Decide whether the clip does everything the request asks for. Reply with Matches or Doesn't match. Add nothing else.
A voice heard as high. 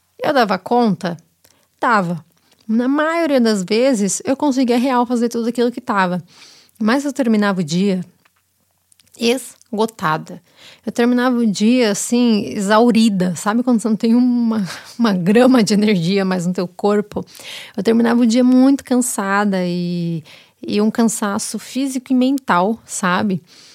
Matches